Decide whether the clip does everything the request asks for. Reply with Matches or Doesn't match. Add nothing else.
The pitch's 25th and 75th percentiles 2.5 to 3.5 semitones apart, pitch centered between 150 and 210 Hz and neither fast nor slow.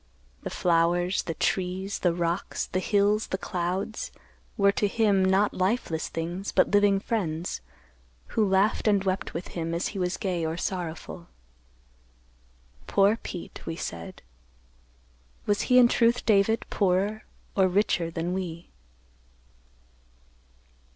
Doesn't match